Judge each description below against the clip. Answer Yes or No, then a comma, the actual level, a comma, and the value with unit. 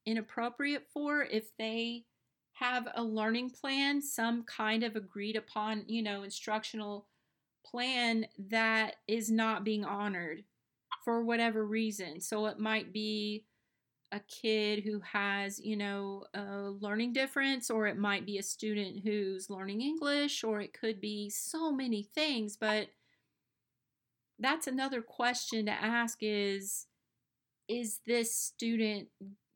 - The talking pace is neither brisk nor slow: No, slow, 130 wpm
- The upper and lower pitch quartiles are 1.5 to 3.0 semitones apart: Yes, narrow, 2.5 semitones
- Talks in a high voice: Yes, high, 220 Hz